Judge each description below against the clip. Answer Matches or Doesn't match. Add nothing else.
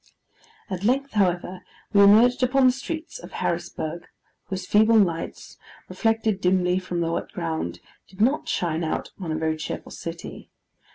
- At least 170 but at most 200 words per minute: Doesn't match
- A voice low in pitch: Doesn't match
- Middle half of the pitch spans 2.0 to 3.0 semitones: Doesn't match